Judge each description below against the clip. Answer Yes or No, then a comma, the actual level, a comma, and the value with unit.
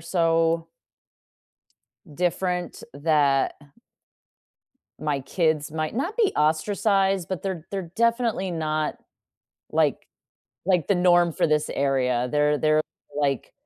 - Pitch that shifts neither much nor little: Yes, average, 3.8 semitones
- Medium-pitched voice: Yes, medium, 165 Hz